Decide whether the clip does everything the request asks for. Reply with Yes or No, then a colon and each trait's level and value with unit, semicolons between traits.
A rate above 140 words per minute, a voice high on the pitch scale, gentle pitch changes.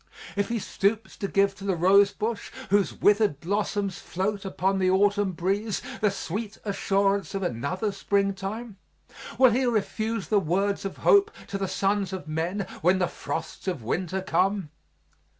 Yes: average, 160 wpm; high, 195 Hz; narrow, 1.6 semitones